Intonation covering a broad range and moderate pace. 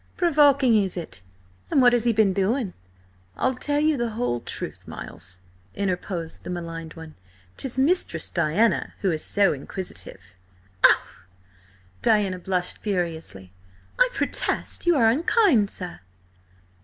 No: wide, 7.0 semitones; slow, 130 wpm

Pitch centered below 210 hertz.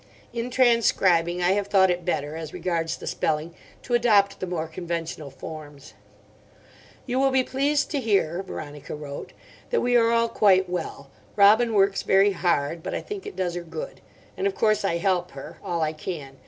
Yes: medium, 185 Hz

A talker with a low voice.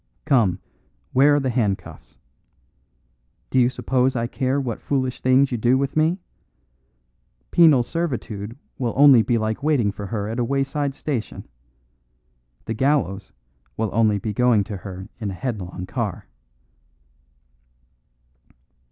Yes: low, 125 Hz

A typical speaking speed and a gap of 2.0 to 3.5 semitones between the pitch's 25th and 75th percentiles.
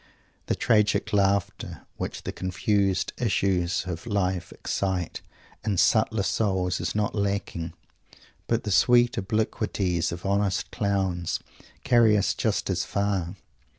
No: slow, 120 wpm; narrow, 2.5 semitones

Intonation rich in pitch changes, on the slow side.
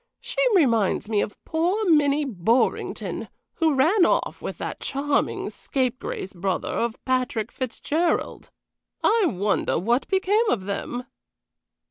Yes: wide, 6.6 semitones; slow, 120 wpm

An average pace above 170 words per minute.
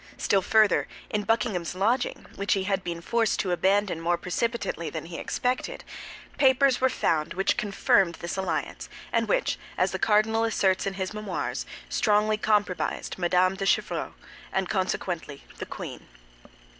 No: average, 150 wpm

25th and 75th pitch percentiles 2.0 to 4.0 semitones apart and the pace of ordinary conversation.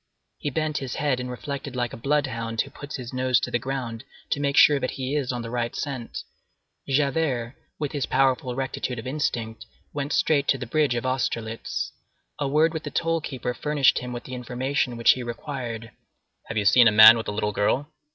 No: average, 3.1 semitones; fast, 210 wpm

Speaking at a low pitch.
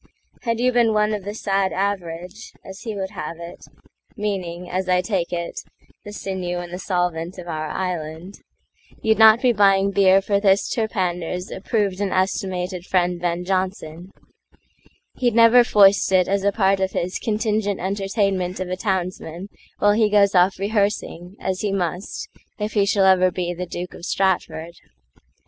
No: high, 190 Hz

